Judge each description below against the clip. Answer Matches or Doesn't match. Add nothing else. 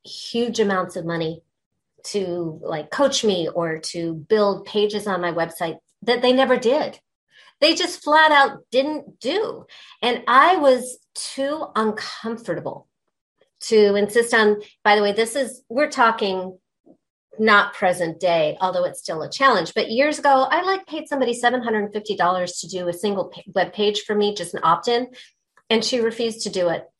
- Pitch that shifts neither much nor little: Doesn't match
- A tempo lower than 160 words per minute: Doesn't match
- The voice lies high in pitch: Matches